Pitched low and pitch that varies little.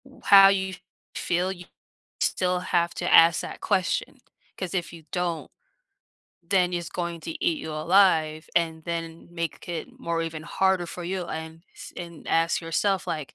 No: medium, 170 Hz; narrow, 1.8 semitones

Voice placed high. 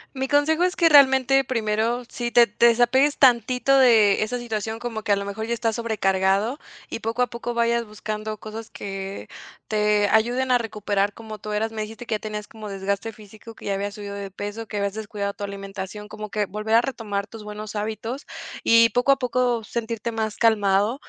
Yes: high, 220 Hz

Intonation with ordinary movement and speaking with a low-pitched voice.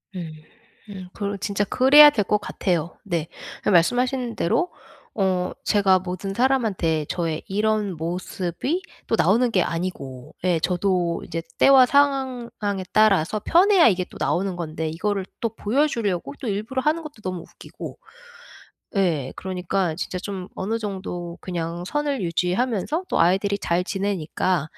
No: average, 4.5 semitones; high, 195 Hz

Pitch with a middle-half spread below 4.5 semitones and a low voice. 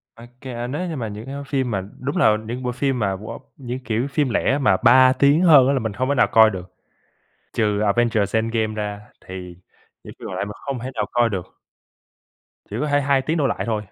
Yes: average, 4.1 semitones; low, 120 Hz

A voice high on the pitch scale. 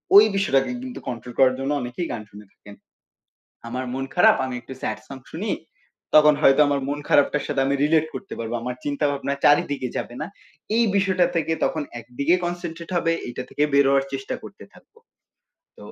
No: medium, 140 Hz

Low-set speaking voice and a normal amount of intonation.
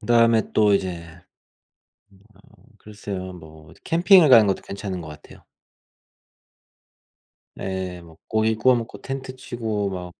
Yes: low, 105 Hz; average, 4.2 semitones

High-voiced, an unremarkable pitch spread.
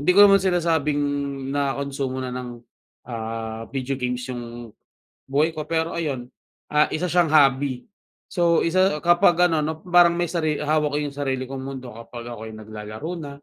No: medium, 145 Hz; average, 4.7 semitones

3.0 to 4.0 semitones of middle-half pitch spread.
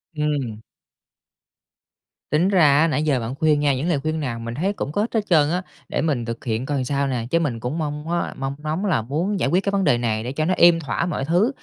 No: average, 4.5 semitones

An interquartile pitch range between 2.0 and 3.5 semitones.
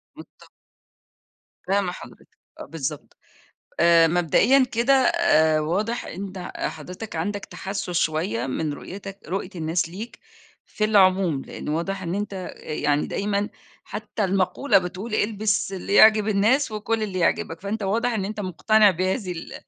No: average, 3.9 semitones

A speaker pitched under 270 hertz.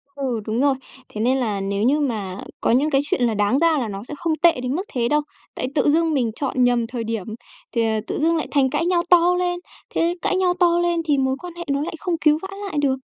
No: very high, 280 Hz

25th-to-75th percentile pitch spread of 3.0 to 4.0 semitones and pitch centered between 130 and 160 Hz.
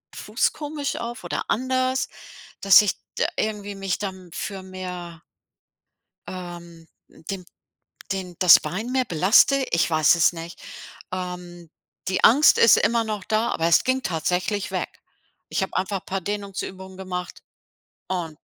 No: average, 3.5 semitones; high, 190 Hz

